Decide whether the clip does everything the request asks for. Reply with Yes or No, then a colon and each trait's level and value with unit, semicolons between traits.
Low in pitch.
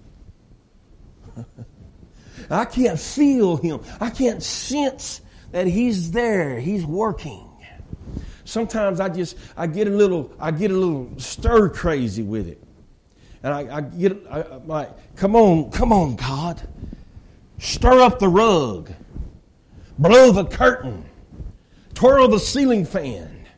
No: medium, 170 Hz